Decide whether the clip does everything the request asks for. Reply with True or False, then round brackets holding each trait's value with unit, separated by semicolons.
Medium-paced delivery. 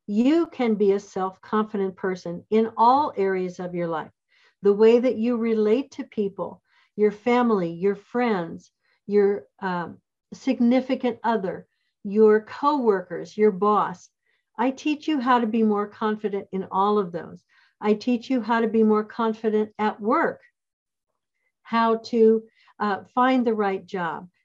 True (150 wpm)